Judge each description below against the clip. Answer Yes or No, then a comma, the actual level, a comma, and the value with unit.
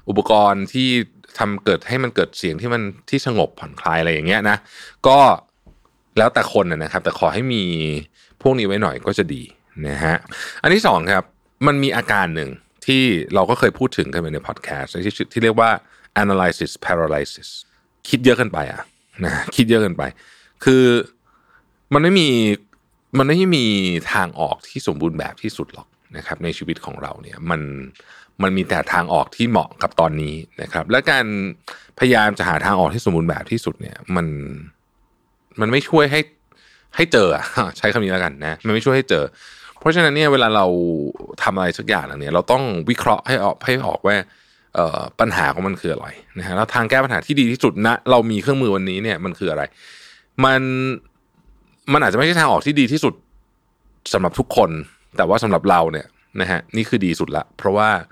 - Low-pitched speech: Yes, low, 110 Hz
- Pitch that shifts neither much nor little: No, wide, 6.3 semitones